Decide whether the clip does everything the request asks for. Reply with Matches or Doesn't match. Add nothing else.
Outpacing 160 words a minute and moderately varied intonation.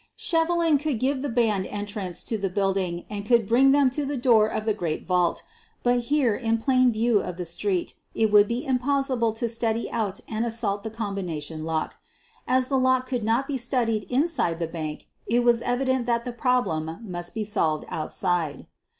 Matches